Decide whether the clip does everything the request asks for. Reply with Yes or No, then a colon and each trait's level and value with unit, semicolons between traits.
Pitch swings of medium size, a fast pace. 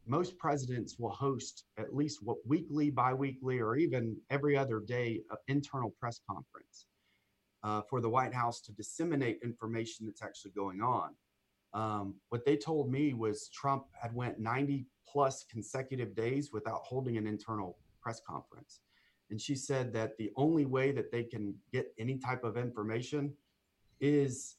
No: average, 4.0 semitones; average, 160 wpm